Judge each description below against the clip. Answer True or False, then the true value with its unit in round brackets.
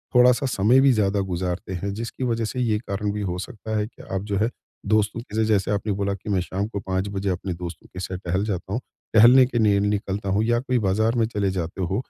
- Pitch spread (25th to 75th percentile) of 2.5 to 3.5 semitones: True (2.9 semitones)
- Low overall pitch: True (105 Hz)